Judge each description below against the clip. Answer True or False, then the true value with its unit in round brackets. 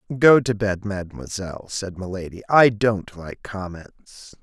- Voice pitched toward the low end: True (100 Hz)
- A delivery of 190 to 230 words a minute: False (135 wpm)